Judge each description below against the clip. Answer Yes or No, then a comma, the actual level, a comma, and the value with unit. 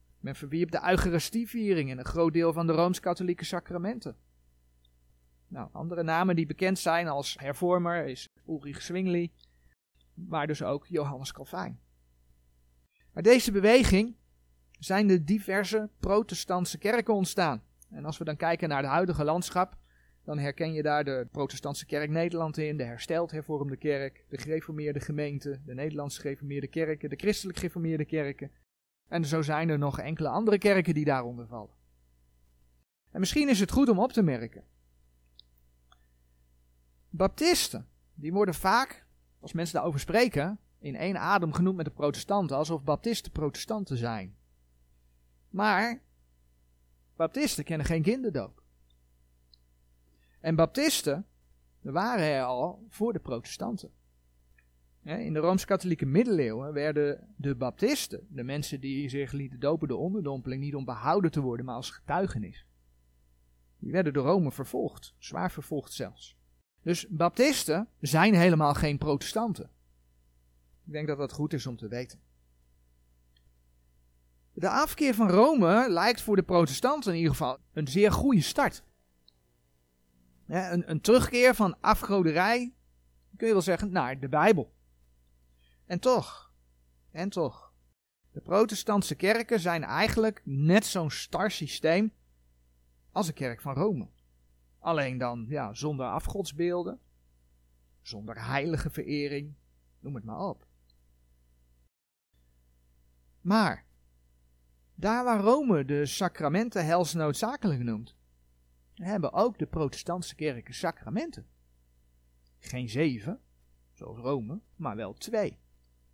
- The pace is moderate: No, slow, 125 wpm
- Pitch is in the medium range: Yes, medium, 145 Hz